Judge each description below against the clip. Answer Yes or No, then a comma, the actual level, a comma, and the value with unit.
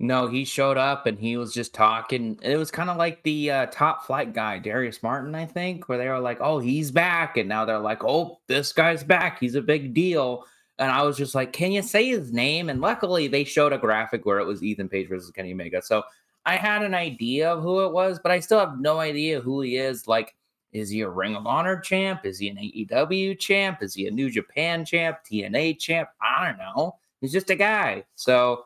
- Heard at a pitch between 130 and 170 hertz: Yes, medium, 140 Hz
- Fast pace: Yes, fast, 235 wpm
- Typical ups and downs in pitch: No, wide, 6.2 semitones